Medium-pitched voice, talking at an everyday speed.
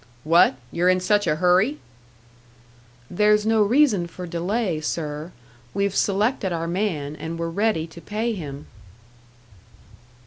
No: medium, 180 Hz; slow, 130 wpm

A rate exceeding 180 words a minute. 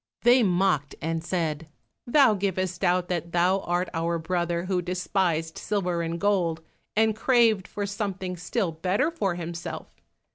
No: average, 145 wpm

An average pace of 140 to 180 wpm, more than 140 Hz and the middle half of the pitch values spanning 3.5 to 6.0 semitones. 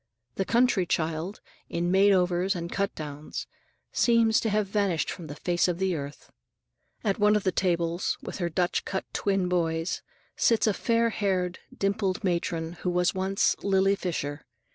No: average, 165 wpm; medium, 185 Hz; average, 2.7 semitones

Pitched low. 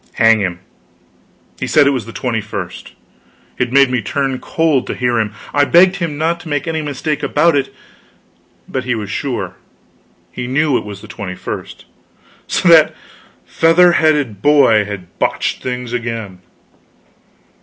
Yes: low, 130 Hz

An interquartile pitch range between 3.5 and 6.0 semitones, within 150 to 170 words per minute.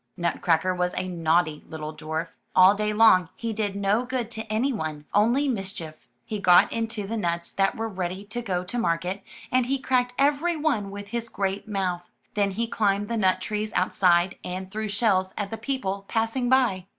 No: average, 3.9 semitones; average, 190 wpm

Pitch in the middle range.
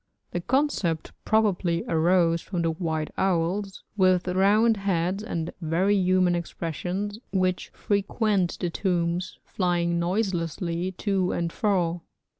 Yes: medium, 180 Hz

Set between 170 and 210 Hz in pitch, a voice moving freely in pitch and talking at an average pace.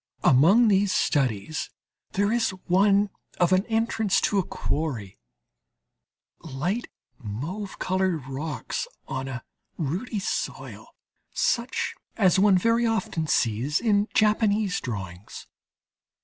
No: medium, 185 Hz; wide, 7.6 semitones; slow, 105 wpm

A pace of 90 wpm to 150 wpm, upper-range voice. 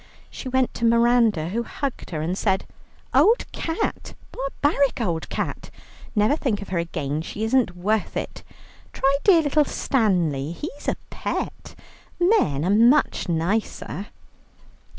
Yes: slow, 135 wpm; high, 220 Hz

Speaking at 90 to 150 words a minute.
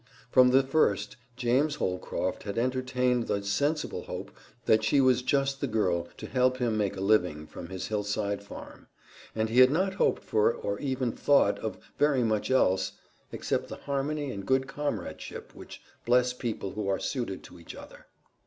No: average, 175 wpm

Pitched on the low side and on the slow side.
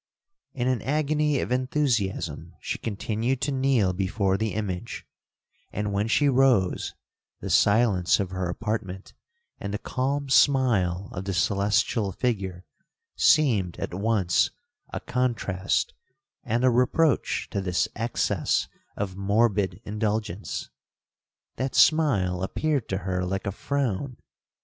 Yes: low, 105 Hz; slow, 125 wpm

